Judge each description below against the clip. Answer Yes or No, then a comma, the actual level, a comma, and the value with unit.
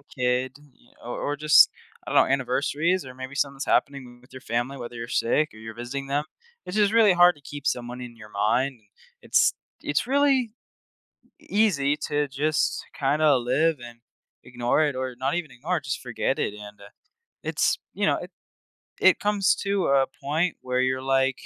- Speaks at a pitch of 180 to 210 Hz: No, low, 135 Hz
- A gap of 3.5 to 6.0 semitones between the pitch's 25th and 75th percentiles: Yes, average, 3.8 semitones